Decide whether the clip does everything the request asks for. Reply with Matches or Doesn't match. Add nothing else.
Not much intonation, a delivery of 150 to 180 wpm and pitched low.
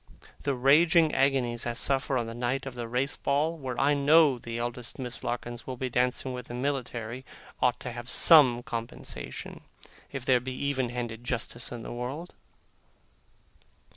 Matches